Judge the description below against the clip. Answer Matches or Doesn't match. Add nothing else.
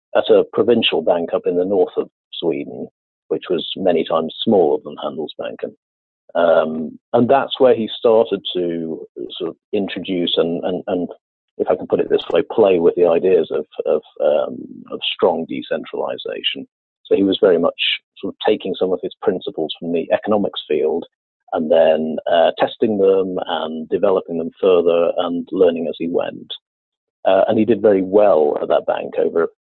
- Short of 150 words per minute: Doesn't match